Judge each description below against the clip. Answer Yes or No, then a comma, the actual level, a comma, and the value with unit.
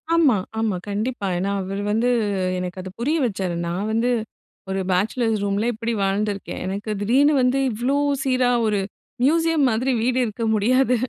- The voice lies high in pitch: Yes, high, 225 Hz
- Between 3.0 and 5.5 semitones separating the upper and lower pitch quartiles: Yes, average, 4.2 semitones